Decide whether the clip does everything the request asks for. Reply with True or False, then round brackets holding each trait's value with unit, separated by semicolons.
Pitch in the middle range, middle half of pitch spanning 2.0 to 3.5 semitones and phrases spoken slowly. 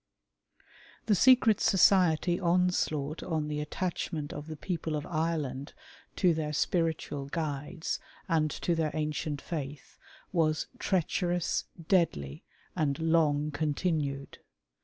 True (155 Hz; 2.8 semitones; 110 wpm)